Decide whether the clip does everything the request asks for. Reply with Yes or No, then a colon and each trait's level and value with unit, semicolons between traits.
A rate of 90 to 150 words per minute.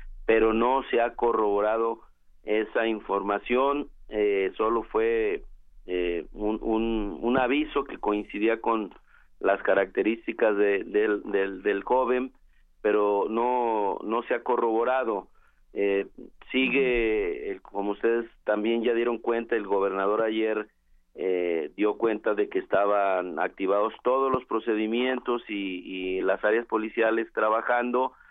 Yes: slow, 125 wpm